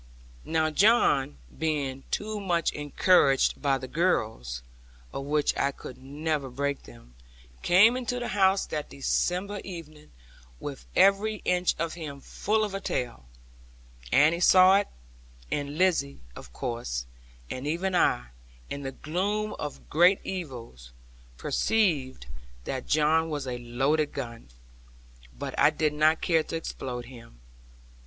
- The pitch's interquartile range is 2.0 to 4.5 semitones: No, wide, 5.6 semitones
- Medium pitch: Yes, medium, 150 Hz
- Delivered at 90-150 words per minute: Yes, slow, 135 wpm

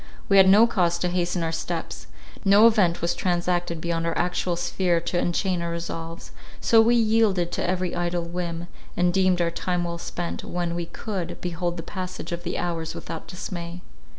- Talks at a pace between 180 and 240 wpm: Yes, average, 185 wpm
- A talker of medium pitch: Yes, medium, 175 Hz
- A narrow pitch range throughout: Yes, narrow, 1.4 semitones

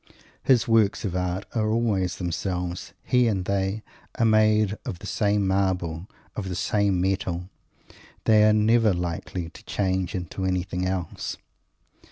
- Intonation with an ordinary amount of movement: Yes, average, 3.0 semitones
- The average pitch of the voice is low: Yes, very low, 95 Hz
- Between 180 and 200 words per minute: No, average, 145 wpm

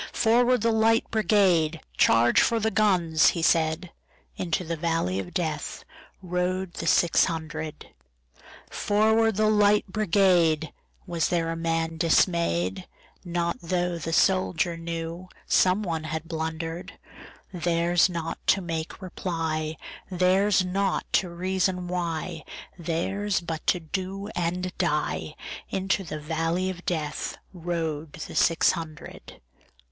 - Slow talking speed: Yes, slow, 100 wpm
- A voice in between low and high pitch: Yes, medium, 170 Hz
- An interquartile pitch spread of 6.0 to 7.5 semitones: No, narrow, 2.6 semitones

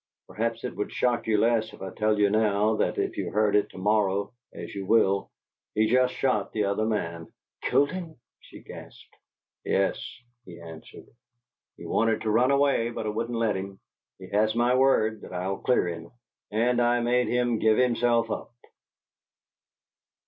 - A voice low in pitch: Yes, low, 110 Hz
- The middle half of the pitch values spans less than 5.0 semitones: Yes, average, 2.9 semitones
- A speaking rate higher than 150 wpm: Yes, average, 175 wpm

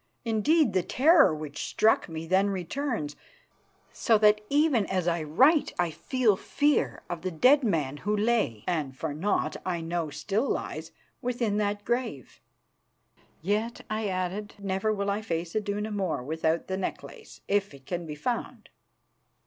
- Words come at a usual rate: Yes, average, 155 wpm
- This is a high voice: Yes, high, 200 Hz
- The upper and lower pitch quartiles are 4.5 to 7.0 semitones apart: Yes, average, 5.1 semitones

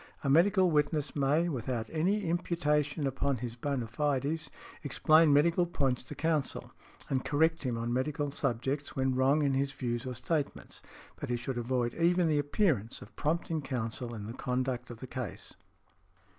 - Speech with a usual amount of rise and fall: Yes, average, 3.7 semitones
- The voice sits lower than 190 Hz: Yes, medium, 140 Hz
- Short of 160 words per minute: No, average, 165 wpm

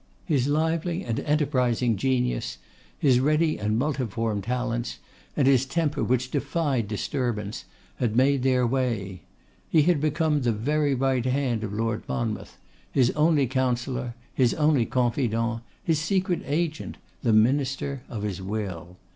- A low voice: Yes, low, 130 Hz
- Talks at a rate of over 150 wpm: No, average, 140 wpm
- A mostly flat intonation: No, average, 4.1 semitones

